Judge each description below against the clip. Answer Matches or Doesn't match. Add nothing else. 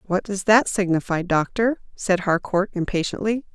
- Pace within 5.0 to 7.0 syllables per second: Doesn't match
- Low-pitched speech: Doesn't match